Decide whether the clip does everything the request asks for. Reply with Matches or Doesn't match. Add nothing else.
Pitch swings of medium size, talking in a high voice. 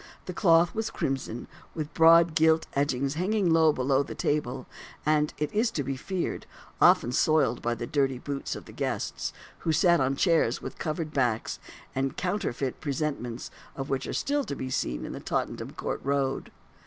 Doesn't match